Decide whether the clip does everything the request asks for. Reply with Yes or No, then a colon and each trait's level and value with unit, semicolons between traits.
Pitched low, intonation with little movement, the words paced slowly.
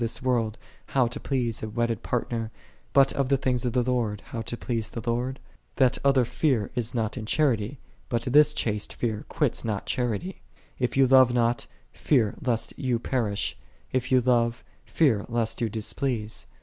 No: low, 120 Hz; narrow, 2.3 semitones; average, 190 wpm